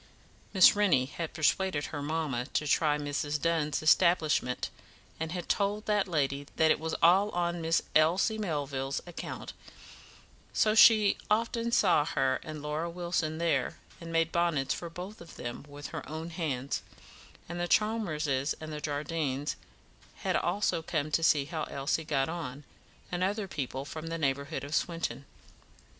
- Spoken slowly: No, average, 155 wpm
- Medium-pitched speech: Yes, medium, 160 Hz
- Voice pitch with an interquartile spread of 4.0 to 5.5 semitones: No, average, 3.3 semitones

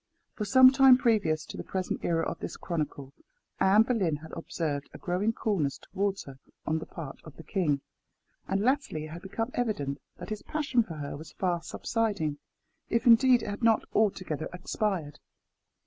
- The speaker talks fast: No, average, 180 wpm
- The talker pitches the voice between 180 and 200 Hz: Yes, high, 190 Hz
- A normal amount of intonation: No, wide, 6.3 semitones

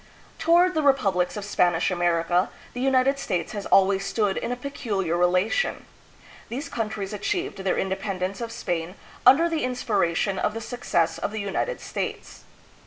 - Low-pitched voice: No, high, 205 Hz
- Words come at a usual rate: Yes, average, 155 wpm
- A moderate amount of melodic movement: No, wide, 5.7 semitones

